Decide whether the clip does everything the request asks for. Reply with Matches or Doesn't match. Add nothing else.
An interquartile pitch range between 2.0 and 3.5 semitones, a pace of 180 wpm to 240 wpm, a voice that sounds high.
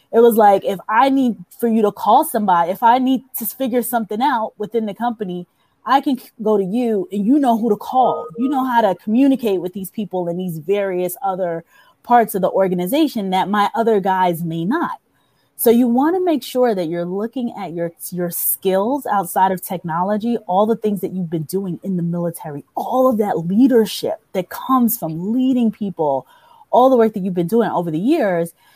Doesn't match